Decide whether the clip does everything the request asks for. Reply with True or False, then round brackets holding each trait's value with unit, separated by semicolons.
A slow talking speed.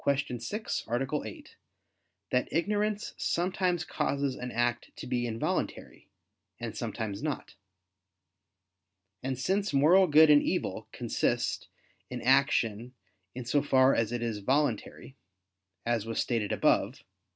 True (125 wpm)